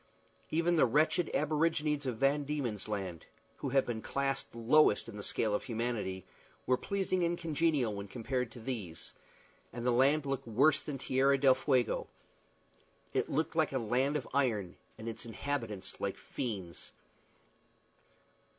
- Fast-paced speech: No, average, 150 wpm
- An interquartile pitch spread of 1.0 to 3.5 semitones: No, average, 4.6 semitones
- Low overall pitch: Yes, low, 130 Hz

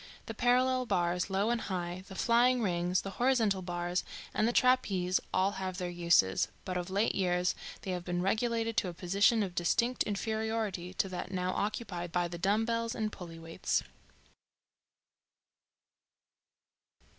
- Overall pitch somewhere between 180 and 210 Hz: Yes, high, 190 Hz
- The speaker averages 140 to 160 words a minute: Yes, average, 150 wpm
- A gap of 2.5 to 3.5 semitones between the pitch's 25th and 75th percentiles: No, average, 4.1 semitones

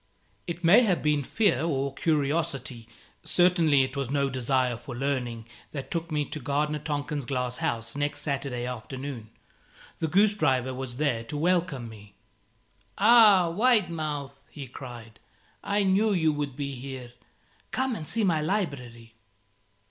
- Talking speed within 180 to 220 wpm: No, average, 150 wpm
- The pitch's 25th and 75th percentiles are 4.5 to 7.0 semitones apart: Yes, average, 4.8 semitones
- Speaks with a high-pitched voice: No, medium, 145 Hz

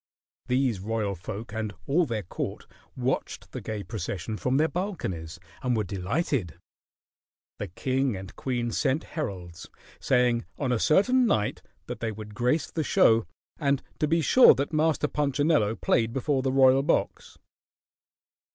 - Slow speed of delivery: No, average, 150 wpm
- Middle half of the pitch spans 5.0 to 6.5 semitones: Yes, wide, 5.6 semitones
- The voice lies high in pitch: No, low, 125 Hz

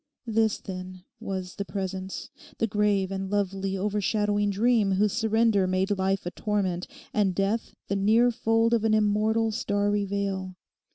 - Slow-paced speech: No, average, 150 wpm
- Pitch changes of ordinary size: No, narrow, 2.2 semitones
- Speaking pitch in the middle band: No, high, 205 Hz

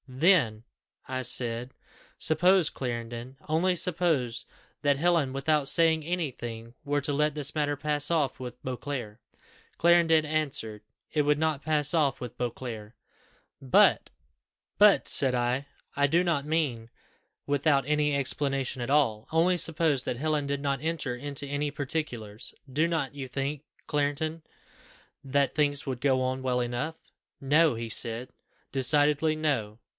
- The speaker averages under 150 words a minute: Yes, average, 140 wpm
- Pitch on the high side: No, medium, 140 Hz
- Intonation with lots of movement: No, average, 3.4 semitones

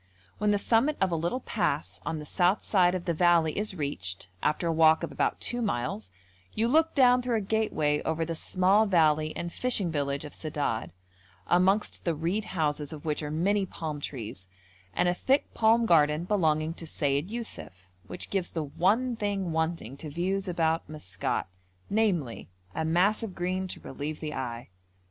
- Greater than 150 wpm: Yes, average, 180 wpm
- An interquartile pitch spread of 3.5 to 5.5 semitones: Yes, average, 4.9 semitones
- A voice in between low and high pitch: Yes, medium, 170 Hz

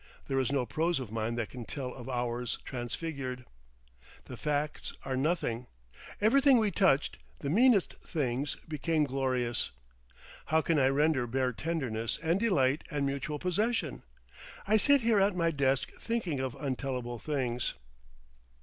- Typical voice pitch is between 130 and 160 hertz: Yes, medium, 140 Hz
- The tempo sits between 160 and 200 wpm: No, average, 145 wpm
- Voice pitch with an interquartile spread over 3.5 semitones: Yes, average, 4.8 semitones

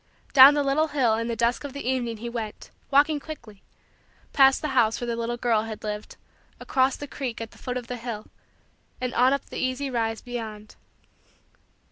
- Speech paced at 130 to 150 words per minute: No, average, 195 wpm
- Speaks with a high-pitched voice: Yes, high, 245 Hz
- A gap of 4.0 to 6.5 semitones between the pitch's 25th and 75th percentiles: No, average, 3.0 semitones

